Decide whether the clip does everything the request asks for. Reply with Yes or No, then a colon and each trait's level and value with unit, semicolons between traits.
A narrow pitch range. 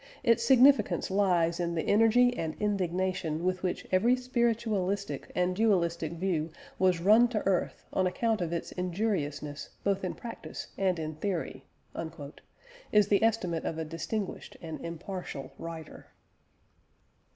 No: average, 4.3 semitones